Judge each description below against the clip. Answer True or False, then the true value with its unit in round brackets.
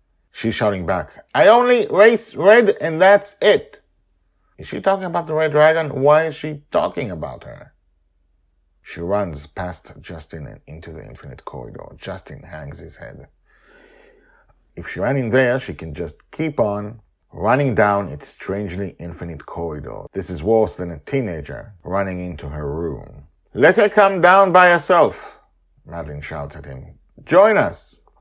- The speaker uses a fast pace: False (155 wpm)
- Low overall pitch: True (105 Hz)